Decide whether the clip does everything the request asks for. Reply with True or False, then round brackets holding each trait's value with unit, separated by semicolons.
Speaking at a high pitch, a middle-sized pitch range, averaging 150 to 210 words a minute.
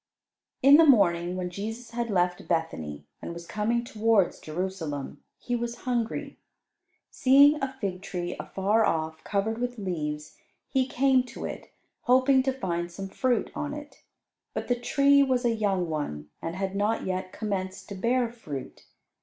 False (210 Hz; 5.8 semitones; 160 wpm)